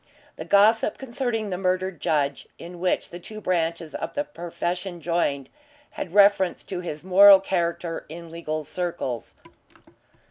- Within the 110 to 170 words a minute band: Yes, average, 140 wpm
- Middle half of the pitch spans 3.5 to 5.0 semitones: No, average, 2.8 semitones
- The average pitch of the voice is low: No, medium, 175 Hz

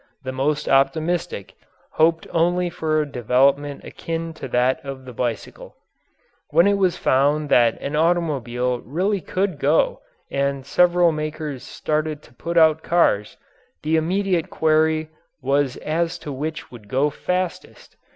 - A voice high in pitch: No, medium, 155 Hz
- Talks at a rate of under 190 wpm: Yes, average, 140 wpm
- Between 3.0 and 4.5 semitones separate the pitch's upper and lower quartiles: Yes, average, 3.7 semitones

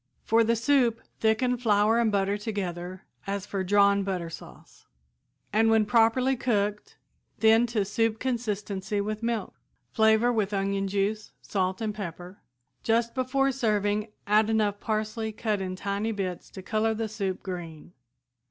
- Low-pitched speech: No, high, 210 Hz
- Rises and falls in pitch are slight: Yes, narrow, 2.2 semitones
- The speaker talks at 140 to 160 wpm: Yes, average, 145 wpm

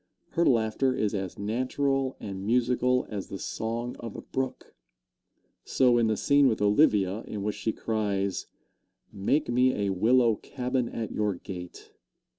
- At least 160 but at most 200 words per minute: No, average, 150 wpm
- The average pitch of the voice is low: Yes, low, 115 Hz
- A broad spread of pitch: No, average, 3.8 semitones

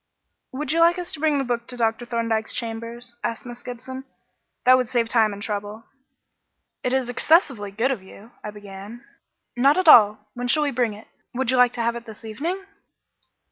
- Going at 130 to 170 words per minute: No, fast, 205 wpm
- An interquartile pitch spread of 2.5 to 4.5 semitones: Yes, average, 2.8 semitones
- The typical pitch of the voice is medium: No, high, 240 Hz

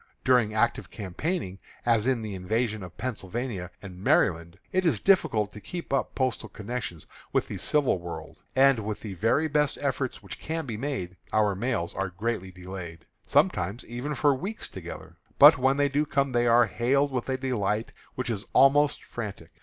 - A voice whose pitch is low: Yes, low, 115 Hz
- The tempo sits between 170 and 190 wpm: Yes, average, 175 wpm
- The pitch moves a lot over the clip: Yes, wide, 5.8 semitones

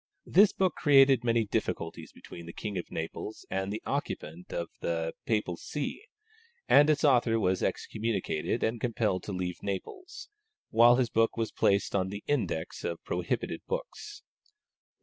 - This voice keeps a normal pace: Yes, average, 150 wpm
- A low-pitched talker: Yes, low, 110 Hz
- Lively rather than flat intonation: Yes, wide, 6.5 semitones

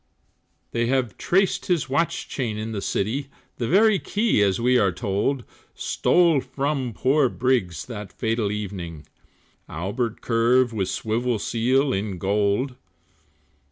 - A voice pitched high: No, low, 120 Hz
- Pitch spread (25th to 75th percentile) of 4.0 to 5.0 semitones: Yes, average, 4.6 semitones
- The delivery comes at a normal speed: No, slow, 130 wpm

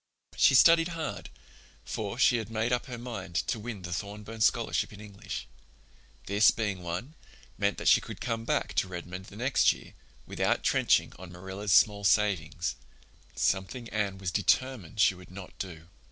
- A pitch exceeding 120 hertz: No, low, 100 Hz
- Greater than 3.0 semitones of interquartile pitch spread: Yes, average, 3.6 semitones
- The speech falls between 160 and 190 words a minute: Yes, average, 165 wpm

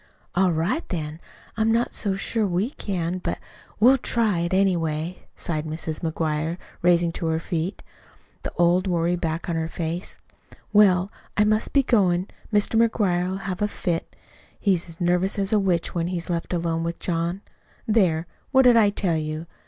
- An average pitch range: Yes, average, 3.4 semitones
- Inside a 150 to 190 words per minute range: Yes, average, 170 wpm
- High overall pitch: No, medium, 175 Hz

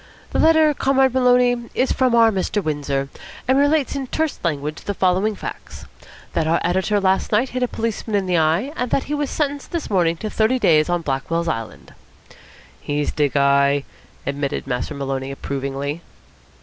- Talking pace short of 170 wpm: No, average, 175 wpm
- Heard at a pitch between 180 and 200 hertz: Yes, high, 190 Hz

